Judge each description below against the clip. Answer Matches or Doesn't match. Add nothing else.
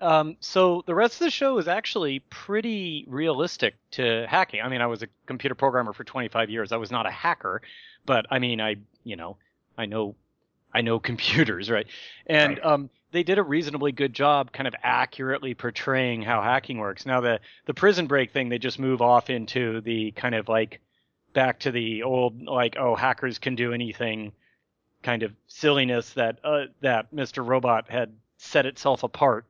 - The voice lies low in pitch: Matches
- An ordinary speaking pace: Matches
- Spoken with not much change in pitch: Doesn't match